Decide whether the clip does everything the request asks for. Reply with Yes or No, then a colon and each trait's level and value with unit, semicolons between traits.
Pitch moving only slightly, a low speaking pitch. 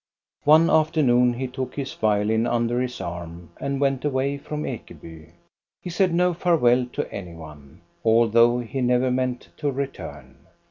No: average, 3.9 semitones; low, 125 Hz